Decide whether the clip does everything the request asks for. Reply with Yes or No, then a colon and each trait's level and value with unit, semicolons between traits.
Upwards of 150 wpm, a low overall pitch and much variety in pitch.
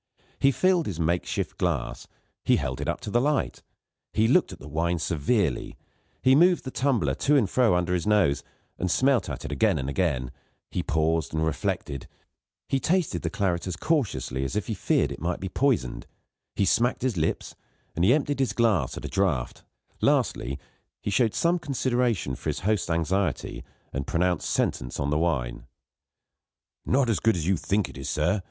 Yes: average, 185 wpm; very low, 95 Hz; wide, 7.7 semitones